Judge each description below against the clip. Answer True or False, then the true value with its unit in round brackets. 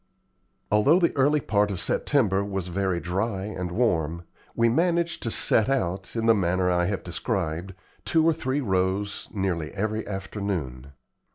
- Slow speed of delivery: False (155 wpm)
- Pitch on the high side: False (100 Hz)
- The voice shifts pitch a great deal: False (4.2 semitones)